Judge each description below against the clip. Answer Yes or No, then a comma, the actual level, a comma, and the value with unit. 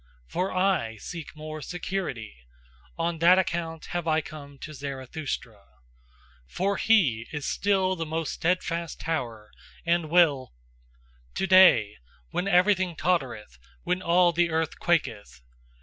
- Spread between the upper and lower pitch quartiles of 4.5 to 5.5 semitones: Yes, average, 4.8 semitones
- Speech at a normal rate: No, slow, 125 wpm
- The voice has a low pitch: No, medium, 165 Hz